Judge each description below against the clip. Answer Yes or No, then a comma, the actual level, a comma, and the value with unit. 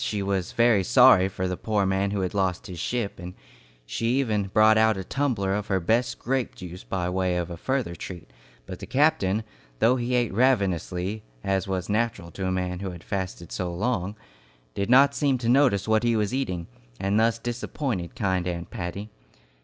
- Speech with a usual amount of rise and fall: Yes, average, 4.3 semitones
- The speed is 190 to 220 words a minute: Yes, average, 195 wpm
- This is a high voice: No, low, 100 Hz